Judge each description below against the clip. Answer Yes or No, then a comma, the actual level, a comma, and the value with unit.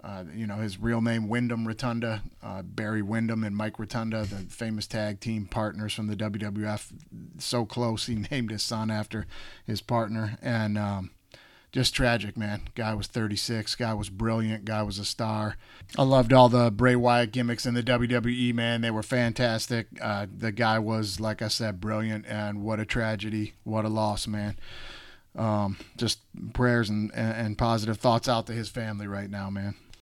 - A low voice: Yes, low, 110 Hz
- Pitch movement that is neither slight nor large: No, narrow, 1.8 semitones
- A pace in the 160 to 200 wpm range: Yes, average, 180 wpm